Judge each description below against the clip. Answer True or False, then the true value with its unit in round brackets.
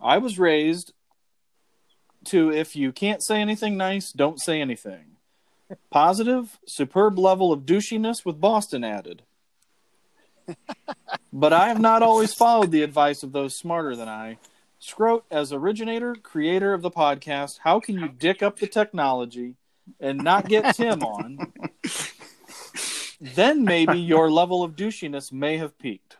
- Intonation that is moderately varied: False (6.6 semitones)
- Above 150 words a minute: False (140 wpm)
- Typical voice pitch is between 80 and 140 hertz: False (180 Hz)